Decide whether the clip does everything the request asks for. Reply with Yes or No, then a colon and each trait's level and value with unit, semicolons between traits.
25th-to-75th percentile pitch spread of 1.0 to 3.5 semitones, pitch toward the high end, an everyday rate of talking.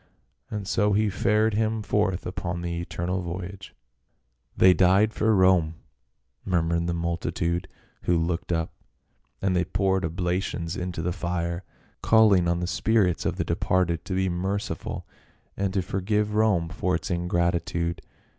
No: narrow, 2.4 semitones; very low, 90 Hz; average, 155 wpm